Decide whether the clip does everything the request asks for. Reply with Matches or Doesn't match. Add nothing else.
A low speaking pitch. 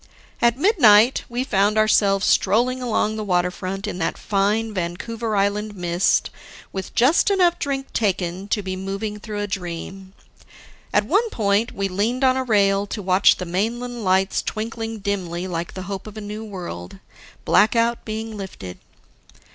Doesn't match